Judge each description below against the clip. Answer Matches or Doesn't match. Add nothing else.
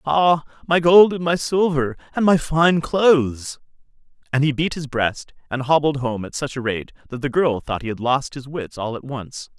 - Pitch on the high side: Doesn't match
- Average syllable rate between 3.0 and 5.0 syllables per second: Matches